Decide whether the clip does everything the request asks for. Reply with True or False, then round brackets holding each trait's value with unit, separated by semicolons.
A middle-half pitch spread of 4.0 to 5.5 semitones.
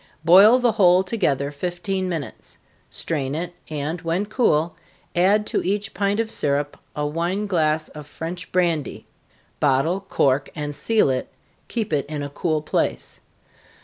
True (4.7 semitones)